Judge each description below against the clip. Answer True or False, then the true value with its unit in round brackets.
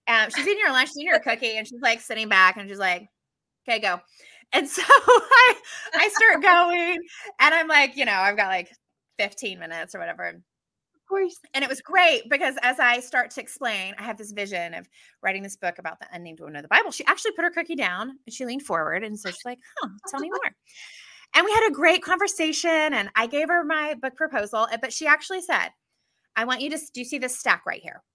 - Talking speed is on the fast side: True (235 wpm)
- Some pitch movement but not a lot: False (7.9 semitones)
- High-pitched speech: True (270 Hz)